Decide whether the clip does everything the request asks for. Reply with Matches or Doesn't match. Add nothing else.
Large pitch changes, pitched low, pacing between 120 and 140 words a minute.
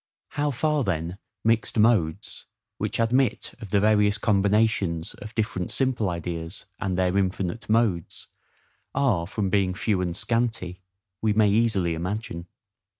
Doesn't match